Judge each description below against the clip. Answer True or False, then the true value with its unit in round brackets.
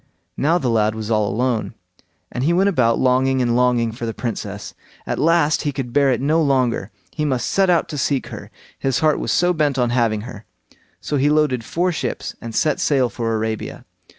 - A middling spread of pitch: True (4.5 semitones)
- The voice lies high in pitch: False (130 Hz)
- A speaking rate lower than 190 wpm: False (205 wpm)